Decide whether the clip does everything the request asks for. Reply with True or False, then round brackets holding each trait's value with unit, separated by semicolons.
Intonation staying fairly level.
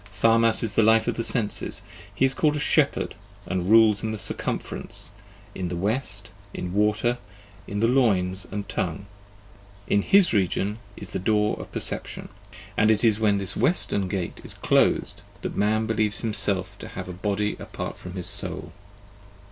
True (2.3 semitones)